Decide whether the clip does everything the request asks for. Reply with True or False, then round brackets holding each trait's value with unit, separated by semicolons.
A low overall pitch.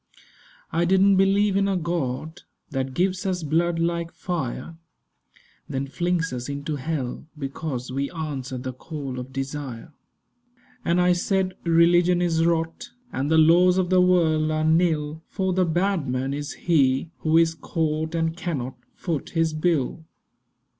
False (160 Hz)